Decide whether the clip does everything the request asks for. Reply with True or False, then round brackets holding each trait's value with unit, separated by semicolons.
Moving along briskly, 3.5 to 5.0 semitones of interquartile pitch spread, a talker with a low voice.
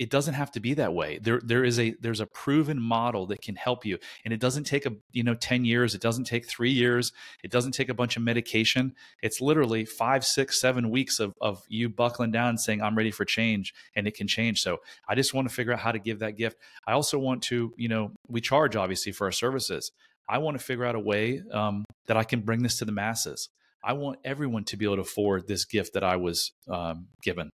False (250 wpm; 2.7 semitones; 115 Hz)